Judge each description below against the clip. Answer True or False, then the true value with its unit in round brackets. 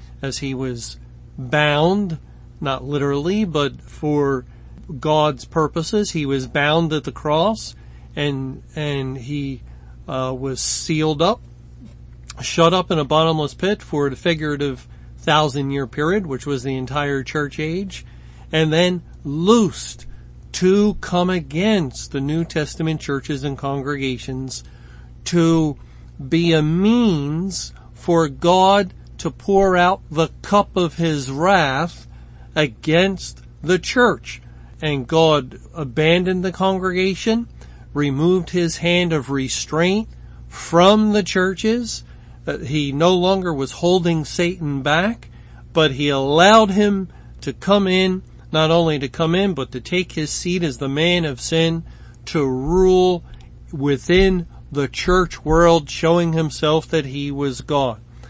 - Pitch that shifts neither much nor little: True (4.8 semitones)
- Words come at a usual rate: False (130 wpm)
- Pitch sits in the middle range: True (155 Hz)